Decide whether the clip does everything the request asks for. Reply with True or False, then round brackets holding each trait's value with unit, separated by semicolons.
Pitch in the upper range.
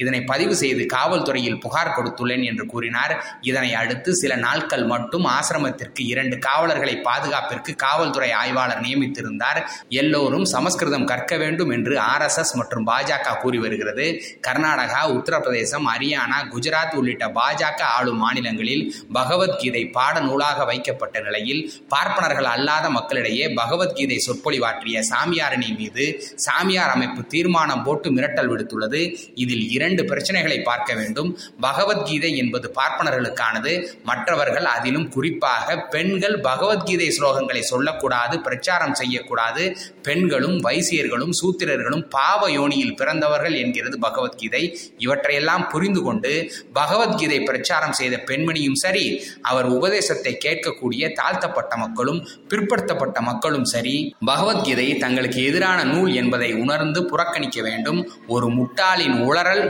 False (135 Hz)